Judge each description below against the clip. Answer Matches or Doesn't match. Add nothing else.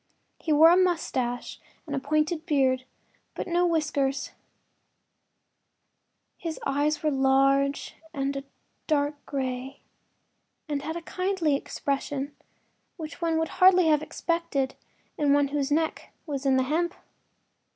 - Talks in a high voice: Matches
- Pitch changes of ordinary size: Matches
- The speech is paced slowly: Matches